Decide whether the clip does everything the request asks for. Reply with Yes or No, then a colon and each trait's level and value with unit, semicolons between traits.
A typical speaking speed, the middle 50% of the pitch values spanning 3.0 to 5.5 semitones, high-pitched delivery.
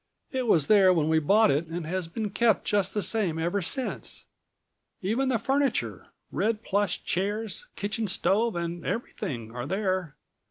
Yes: average, 160 wpm; average, 4.6 semitones; high, 200 Hz